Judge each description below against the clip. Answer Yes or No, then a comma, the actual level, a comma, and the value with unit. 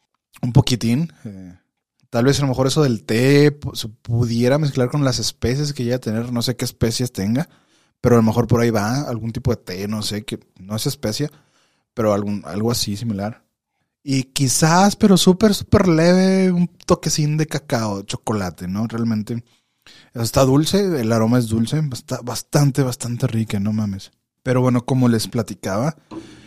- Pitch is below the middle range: Yes, low, 125 Hz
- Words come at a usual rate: Yes, average, 180 wpm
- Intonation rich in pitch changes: No, average, 4.3 semitones